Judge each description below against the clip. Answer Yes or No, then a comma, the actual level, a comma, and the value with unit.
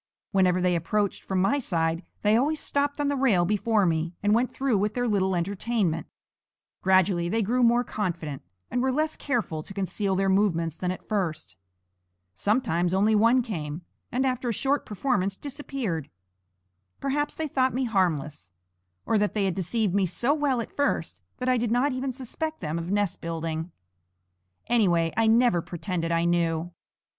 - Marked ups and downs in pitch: Yes, wide, 6.2 semitones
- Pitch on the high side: Yes, high, 205 Hz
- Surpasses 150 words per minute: Yes, average, 170 wpm